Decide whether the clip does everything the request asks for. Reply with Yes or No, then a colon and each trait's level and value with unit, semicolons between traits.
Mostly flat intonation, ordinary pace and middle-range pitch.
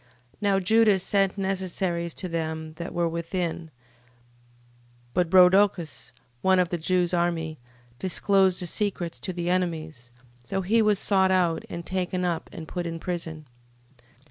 Yes: narrow, 2.2 semitones; average, 150 wpm; medium, 180 Hz